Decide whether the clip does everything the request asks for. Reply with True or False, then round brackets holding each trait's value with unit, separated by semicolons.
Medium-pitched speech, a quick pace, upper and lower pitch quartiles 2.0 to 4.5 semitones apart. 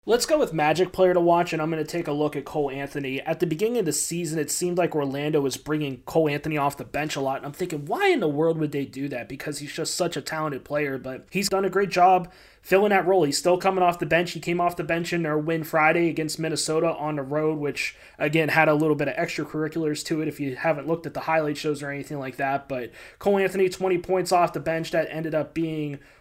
True (155 Hz; 270 wpm; 2.9 semitones)